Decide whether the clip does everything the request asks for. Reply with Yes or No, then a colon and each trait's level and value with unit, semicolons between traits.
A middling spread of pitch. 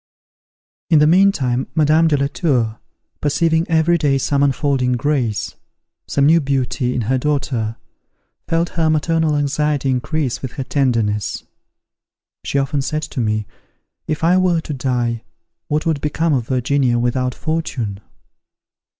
Yes: average, 3.8 semitones